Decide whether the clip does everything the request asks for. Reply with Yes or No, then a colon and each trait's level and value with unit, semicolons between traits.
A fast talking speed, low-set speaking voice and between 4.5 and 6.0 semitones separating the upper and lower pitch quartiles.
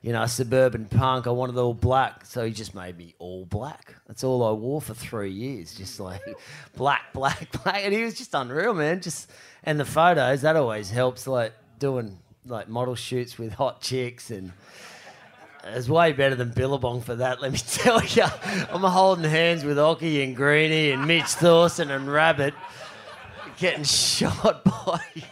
No: average, 180 wpm; low, 130 Hz; average, 4.8 semitones